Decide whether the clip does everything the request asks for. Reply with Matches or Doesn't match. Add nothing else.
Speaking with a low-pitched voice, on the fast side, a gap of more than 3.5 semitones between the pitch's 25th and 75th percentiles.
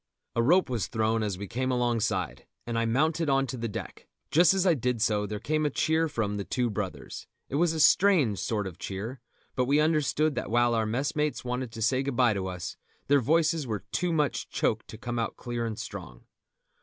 Matches